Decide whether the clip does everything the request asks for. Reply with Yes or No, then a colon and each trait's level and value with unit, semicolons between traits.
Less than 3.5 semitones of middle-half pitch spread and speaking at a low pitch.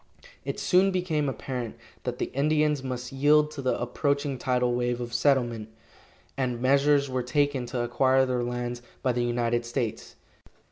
Yes: average, 2.7 semitones; low, 130 Hz